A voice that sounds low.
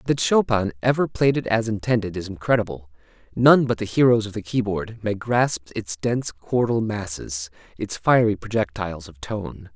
Yes: low, 105 Hz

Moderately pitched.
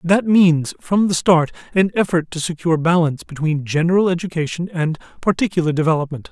Yes: medium, 170 Hz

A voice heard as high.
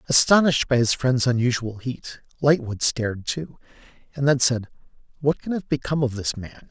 No: low, 130 Hz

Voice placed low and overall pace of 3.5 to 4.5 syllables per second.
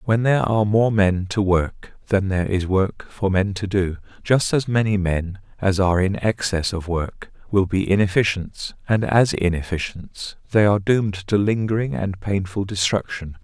No: low, 100 Hz; 4.8 syllables/s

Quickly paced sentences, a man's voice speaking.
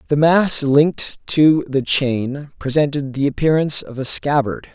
No: average, 150 wpm; male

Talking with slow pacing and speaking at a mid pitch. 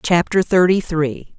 Yes: slow, 130 wpm; medium, 170 Hz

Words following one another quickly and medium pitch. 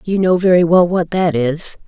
Yes: fast, 225 wpm; medium, 175 Hz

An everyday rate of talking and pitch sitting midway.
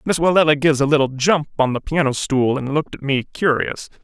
No: fast, 225 wpm; medium, 145 Hz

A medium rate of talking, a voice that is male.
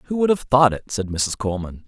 No: fast, 255 wpm; male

